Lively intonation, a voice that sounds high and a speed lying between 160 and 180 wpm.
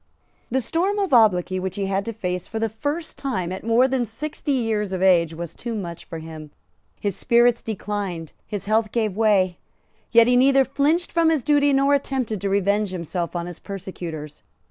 No: wide, 5.9 semitones; high, 215 Hz; average, 190 wpm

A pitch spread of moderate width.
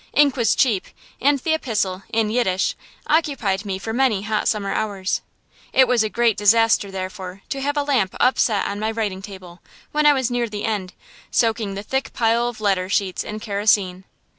Yes: average, 3.9 semitones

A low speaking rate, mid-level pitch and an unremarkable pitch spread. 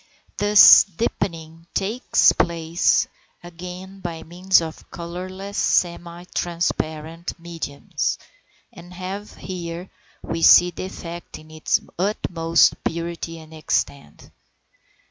No: slow, 95 wpm; medium, 170 Hz; narrow, 2.0 semitones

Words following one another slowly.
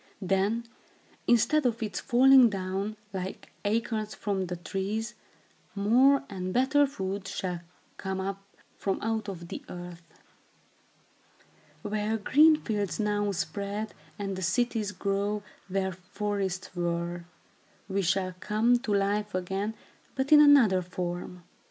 Yes: slow, 125 wpm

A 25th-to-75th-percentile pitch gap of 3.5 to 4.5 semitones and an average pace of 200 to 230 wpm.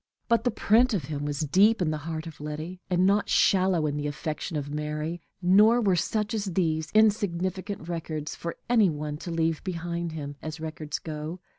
No: average, 3.9 semitones; average, 190 wpm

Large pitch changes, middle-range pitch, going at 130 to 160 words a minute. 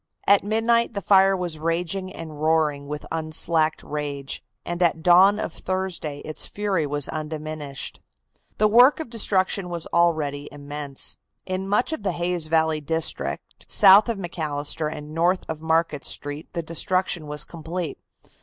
No: average, 3.7 semitones; medium, 165 Hz; average, 150 wpm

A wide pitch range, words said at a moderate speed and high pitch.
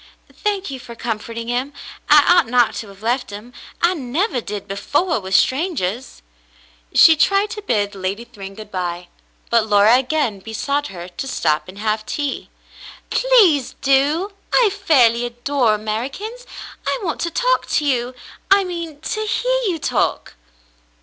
Yes: wide, 7.9 semitones; average, 155 wpm; very high, 255 Hz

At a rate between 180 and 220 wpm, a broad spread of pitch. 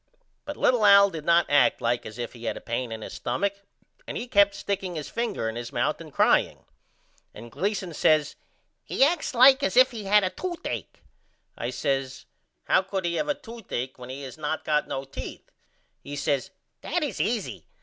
Yes: average, 200 wpm; wide, 7.8 semitones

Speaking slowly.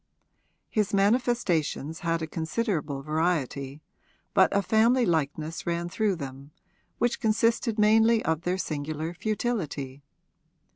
Yes: slow, 110 wpm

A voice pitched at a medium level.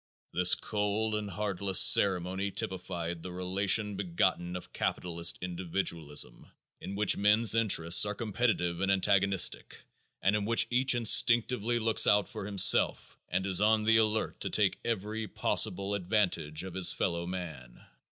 No: low, 100 Hz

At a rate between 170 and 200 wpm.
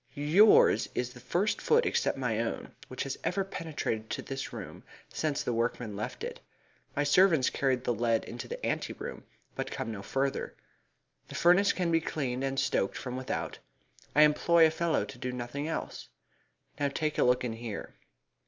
Yes: average, 180 wpm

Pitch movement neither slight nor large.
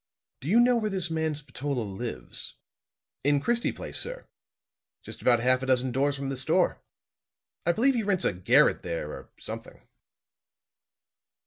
No: wide, 7.8 semitones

